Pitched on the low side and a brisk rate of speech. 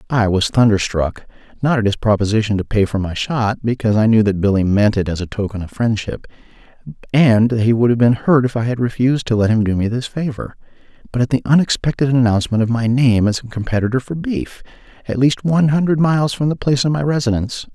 Yes: low, 120 Hz; fast, 225 wpm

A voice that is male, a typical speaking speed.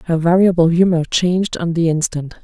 No: female; average, 170 wpm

